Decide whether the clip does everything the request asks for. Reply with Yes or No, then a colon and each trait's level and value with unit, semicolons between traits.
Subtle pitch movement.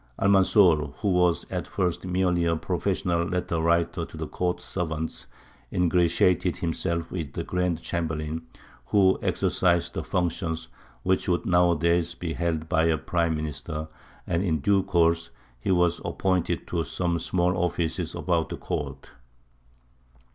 Yes: narrow, 1.7 semitones